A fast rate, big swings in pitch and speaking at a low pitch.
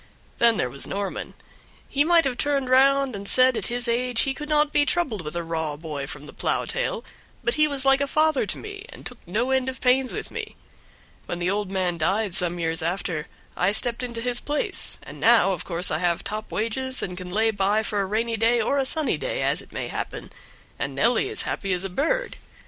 No: fast, 235 wpm; wide, 6.6 semitones; high, 230 Hz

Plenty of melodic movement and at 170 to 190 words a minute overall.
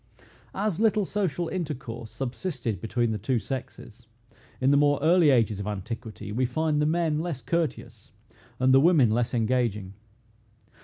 No: wide, 5.8 semitones; average, 150 wpm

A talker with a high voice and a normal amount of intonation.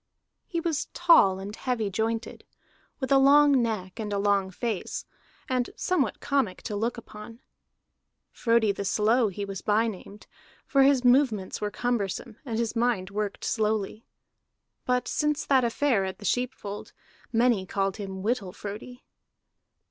Yes: high, 225 Hz; average, 3.7 semitones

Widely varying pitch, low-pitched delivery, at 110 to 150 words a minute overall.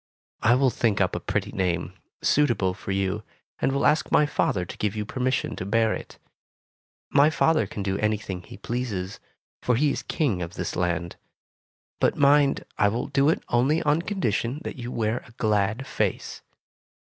No: wide, 6.0 semitones; low, 115 Hz; average, 180 wpm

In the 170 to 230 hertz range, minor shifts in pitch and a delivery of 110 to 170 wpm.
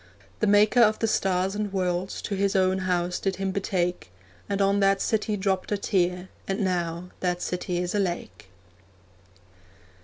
Yes: high, 190 Hz; narrow, 1.9 semitones; average, 165 wpm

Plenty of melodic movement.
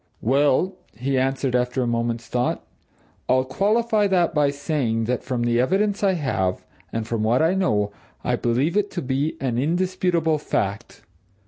Yes: wide, 6.5 semitones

